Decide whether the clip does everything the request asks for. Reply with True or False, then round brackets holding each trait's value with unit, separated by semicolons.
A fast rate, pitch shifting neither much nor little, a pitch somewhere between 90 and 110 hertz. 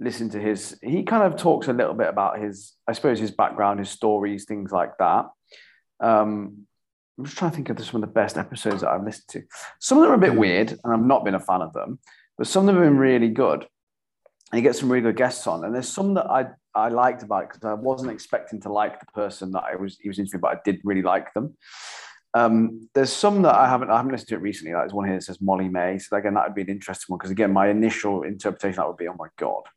True (270 wpm; 3.4 semitones; 105 Hz)